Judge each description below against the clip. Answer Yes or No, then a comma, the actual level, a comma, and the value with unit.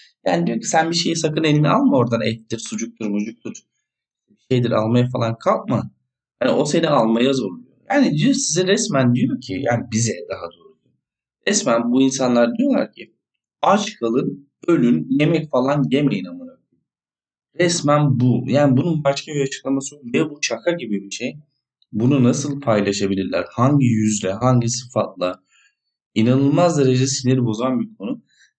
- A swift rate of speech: Yes, fast, 150 wpm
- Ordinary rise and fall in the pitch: Yes, average, 4.7 semitones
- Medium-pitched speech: No, low, 130 Hz